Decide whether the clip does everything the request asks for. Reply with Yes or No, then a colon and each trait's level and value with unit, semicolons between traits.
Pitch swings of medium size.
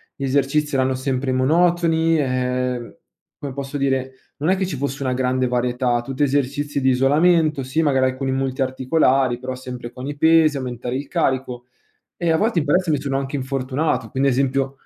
No: narrow, 2.2 semitones